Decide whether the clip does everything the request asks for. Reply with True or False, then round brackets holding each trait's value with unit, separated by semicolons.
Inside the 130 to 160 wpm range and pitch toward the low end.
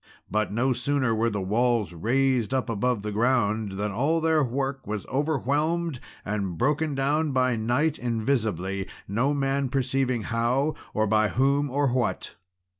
True (150 wpm; 125 Hz)